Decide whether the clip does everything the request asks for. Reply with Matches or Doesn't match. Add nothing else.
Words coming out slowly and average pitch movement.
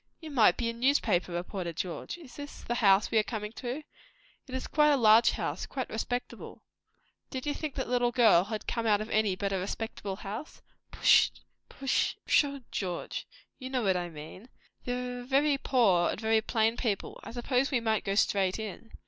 Doesn't match